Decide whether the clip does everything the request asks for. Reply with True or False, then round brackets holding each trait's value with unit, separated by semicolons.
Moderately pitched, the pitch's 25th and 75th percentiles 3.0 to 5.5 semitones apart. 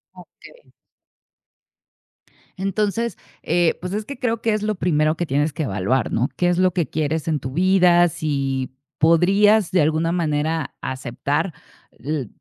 True (165 Hz; 4.3 semitones)